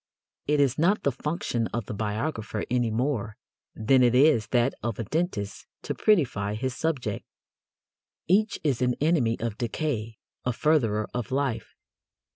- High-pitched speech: No, low, 125 Hz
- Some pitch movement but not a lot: Yes, average, 5.0 semitones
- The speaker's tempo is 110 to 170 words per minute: Yes, average, 150 wpm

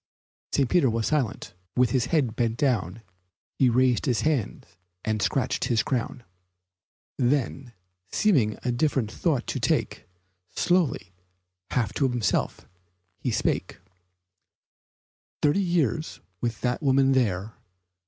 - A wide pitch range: No, average, 3.6 semitones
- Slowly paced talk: Yes, slow, 115 wpm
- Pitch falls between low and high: No, low, 125 Hz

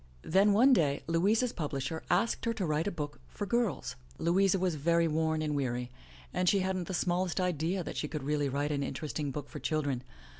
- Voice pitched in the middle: Yes, medium, 165 Hz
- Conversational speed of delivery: No, fast, 210 wpm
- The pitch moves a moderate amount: Yes, average, 4.3 semitones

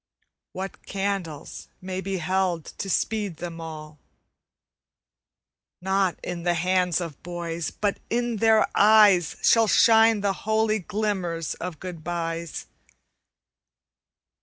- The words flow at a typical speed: No, slow, 110 wpm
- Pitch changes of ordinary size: Yes, average, 3.4 semitones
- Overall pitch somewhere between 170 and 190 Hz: Yes, medium, 185 Hz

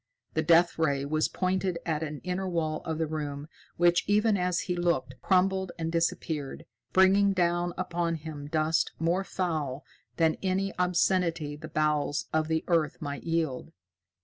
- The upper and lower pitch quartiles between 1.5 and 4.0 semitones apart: Yes, average, 2.8 semitones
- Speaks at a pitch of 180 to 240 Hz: No, medium, 165 Hz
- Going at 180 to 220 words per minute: No, average, 155 wpm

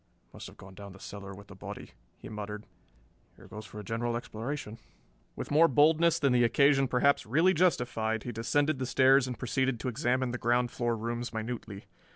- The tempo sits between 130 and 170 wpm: No, average, 190 wpm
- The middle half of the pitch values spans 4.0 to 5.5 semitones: No, average, 3.6 semitones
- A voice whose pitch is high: No, low, 120 Hz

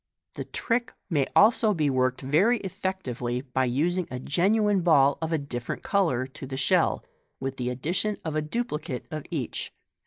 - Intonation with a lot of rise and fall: Yes, wide, 6.3 semitones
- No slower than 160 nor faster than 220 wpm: Yes, average, 165 wpm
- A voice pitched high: No, medium, 150 Hz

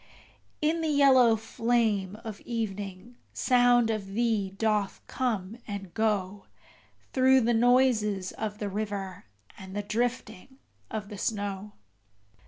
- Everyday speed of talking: No, slow, 120 wpm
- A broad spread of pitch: No, average, 3.2 semitones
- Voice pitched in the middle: No, high, 215 Hz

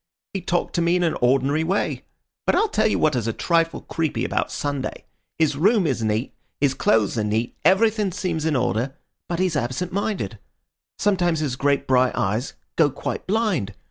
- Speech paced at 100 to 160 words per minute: No, average, 185 wpm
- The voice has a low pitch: No, medium, 155 Hz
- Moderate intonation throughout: No, wide, 6.2 semitones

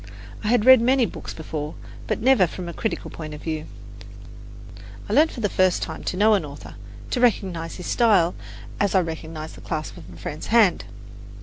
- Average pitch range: No, wide, 6.0 semitones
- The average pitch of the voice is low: No, medium, 185 Hz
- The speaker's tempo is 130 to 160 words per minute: No, average, 195 wpm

